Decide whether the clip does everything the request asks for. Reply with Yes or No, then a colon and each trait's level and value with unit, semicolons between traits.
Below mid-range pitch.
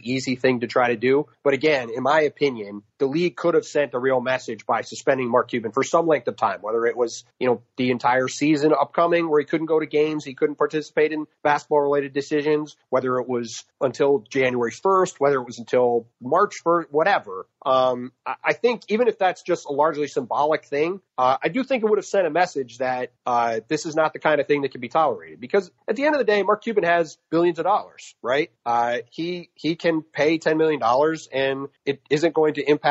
No: medium, 150 Hz